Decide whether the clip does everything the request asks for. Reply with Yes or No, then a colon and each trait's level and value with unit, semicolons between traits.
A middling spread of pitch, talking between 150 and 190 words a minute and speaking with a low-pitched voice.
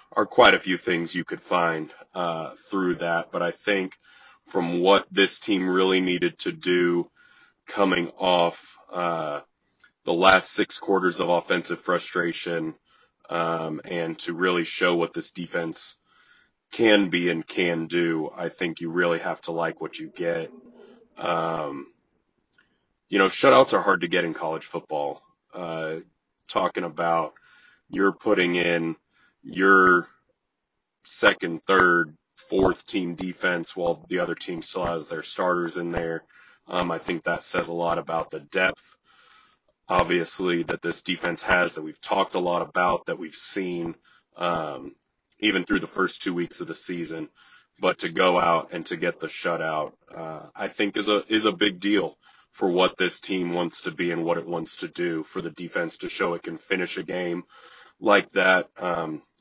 No: narrow, 1.3 semitones; average, 170 wpm; very low, 85 Hz